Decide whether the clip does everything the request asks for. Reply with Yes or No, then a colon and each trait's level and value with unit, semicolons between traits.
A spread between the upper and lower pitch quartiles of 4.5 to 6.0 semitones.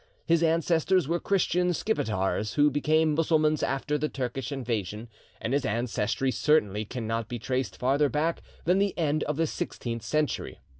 Yes: average, 5.3 semitones